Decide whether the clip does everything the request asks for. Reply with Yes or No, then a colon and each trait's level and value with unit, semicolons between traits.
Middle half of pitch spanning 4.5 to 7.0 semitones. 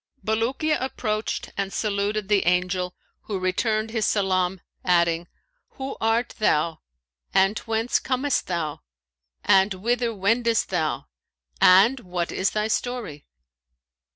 No: average, 3.8 semitones